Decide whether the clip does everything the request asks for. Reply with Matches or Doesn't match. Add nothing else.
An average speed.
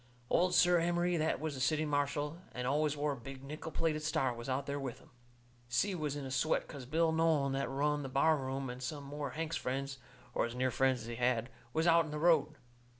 Doesn't match